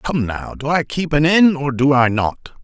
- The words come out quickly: Yes, fast, 250 wpm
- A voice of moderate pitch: Yes, medium, 145 Hz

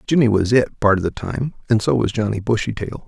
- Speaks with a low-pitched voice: Yes, low, 110 Hz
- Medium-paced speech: No, fast, 235 wpm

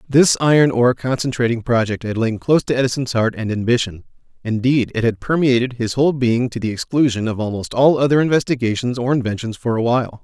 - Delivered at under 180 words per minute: No, average, 190 wpm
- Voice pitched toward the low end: Yes, low, 125 Hz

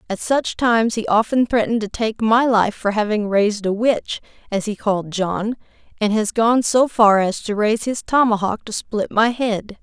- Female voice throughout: Yes, female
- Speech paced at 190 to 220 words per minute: Yes, average, 200 wpm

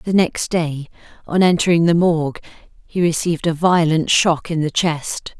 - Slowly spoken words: No, average, 165 wpm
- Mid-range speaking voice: Yes, medium, 165 Hz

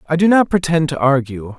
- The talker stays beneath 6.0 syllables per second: Yes, 5.4 syllables/s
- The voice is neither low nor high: Yes, medium, 155 Hz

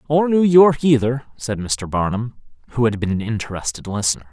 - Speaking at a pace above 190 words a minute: No, average, 180 wpm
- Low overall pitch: Yes, low, 120 Hz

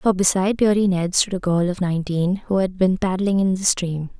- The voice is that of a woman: Yes, female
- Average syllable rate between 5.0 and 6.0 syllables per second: Yes, 5.4 syllables/s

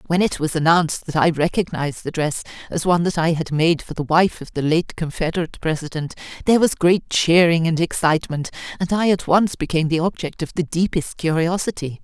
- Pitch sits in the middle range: Yes, medium, 165 Hz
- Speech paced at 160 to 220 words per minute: Yes, average, 200 wpm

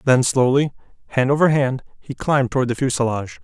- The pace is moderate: Yes, average, 175 wpm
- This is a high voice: No, low, 130 Hz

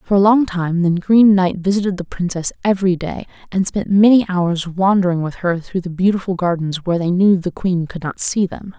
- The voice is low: No, medium, 185 Hz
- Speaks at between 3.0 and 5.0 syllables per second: No, 5.3 syllables/s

